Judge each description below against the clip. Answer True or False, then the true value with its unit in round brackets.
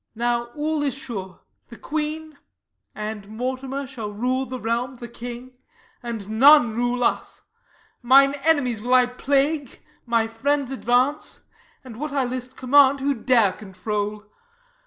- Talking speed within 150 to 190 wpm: False (135 wpm)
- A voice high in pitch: True (250 Hz)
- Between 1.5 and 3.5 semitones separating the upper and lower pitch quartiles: True (3.1 semitones)